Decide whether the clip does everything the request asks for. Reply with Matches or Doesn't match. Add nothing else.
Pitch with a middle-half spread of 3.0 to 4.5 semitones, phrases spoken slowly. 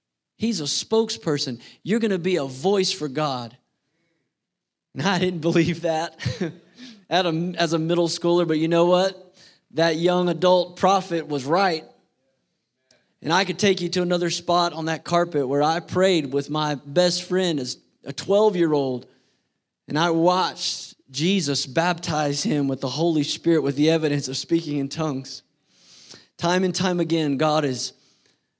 Doesn't match